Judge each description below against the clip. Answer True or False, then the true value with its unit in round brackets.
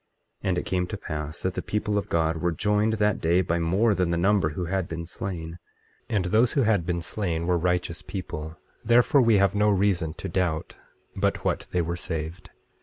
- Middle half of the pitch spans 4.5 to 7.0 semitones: False (3.6 semitones)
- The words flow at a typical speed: False (210 wpm)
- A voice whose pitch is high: False (90 Hz)